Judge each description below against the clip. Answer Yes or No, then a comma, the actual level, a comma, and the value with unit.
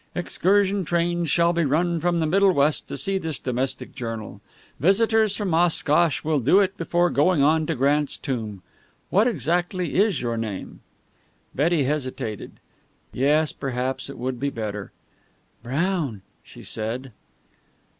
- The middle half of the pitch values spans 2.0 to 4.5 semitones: No, average, 5.3 semitones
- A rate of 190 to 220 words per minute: No, average, 140 wpm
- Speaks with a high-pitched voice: No, medium, 155 Hz